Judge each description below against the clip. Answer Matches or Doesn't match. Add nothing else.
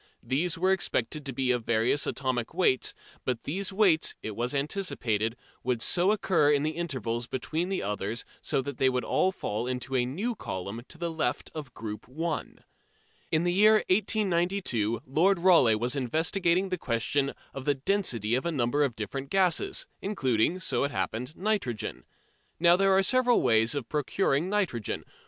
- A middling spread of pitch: Doesn't match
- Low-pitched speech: Doesn't match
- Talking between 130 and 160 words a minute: Doesn't match